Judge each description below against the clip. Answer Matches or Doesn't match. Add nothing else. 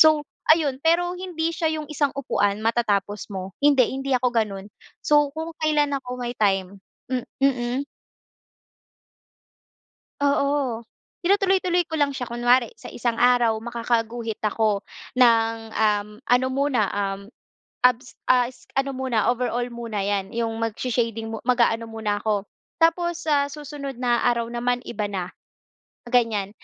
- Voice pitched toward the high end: Matches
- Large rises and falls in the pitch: Doesn't match